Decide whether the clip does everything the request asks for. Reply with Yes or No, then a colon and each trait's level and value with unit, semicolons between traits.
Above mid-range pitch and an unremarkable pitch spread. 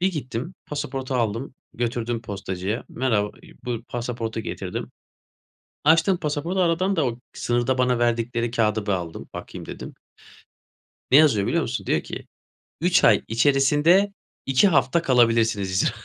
No: low, 125 Hz; average, 4.5 semitones